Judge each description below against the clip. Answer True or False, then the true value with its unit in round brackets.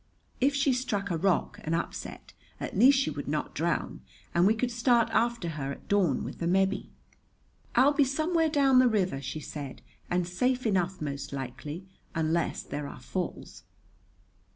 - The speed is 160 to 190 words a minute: True (170 wpm)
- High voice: True (195 Hz)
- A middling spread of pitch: False (8.0 semitones)